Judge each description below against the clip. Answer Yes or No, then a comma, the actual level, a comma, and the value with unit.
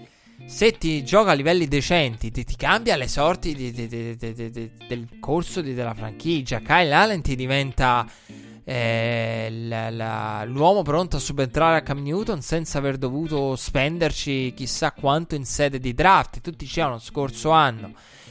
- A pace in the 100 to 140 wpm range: No, average, 165 wpm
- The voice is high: No, medium, 140 Hz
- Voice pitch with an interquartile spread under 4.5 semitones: No, average, 5.3 semitones